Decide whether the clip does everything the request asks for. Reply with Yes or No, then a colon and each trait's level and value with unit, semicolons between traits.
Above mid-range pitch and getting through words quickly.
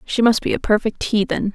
Yes: high, 215 Hz; fast, 235 wpm